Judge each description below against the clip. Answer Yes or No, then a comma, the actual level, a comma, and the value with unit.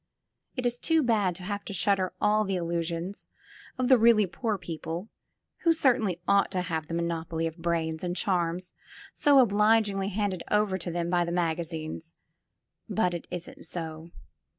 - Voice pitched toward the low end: No, medium, 180 Hz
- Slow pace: No, average, 165 wpm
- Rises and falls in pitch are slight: No, average, 3.9 semitones